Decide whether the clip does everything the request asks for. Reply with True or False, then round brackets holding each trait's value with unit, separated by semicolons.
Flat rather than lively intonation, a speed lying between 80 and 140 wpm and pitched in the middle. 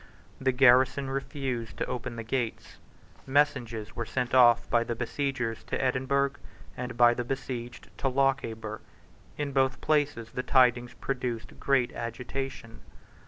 False (2.3 semitones; 135 wpm; 125 Hz)